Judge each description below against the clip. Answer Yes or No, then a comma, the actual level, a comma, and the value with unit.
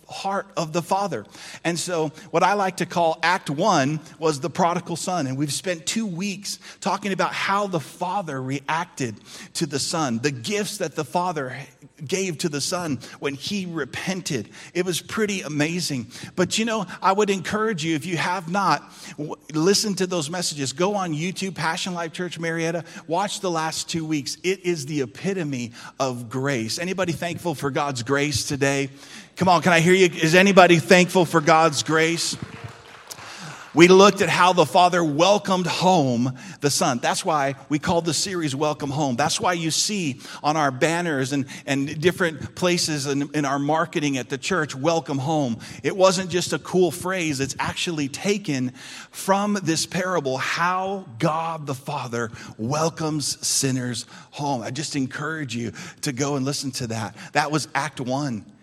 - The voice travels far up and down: No, average, 4.3 semitones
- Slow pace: No, average, 175 wpm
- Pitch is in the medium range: Yes, medium, 160 Hz